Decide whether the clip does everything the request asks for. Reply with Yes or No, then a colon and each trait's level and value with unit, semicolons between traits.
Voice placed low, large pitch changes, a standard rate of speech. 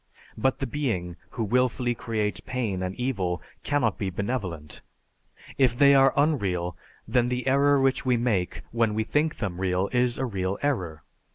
Yes: low, 120 Hz; wide, 5.8 semitones; average, 165 wpm